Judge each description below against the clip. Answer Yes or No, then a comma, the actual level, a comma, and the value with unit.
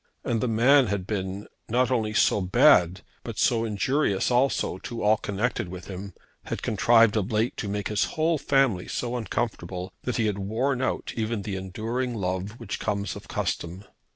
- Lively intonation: No, average, 3.8 semitones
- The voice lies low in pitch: Yes, low, 110 Hz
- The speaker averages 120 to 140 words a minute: No, average, 180 wpm